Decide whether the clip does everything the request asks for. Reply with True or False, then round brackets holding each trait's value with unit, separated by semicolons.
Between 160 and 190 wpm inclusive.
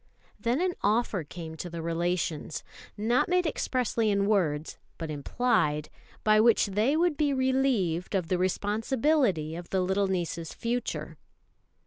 False (140 wpm)